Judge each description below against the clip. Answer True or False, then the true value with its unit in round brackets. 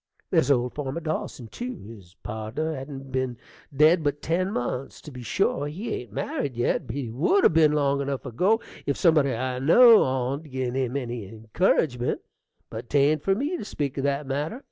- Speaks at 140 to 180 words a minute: False (190 wpm)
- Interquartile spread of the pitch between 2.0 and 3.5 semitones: False (3.9 semitones)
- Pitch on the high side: False (140 Hz)